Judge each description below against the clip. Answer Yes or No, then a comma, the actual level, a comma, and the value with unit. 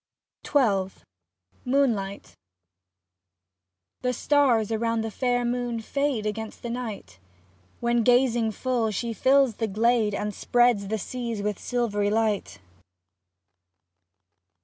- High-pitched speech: Yes, high, 230 Hz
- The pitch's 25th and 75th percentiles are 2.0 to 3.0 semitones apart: Yes, average, 2.7 semitones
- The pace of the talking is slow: Yes, slow, 105 wpm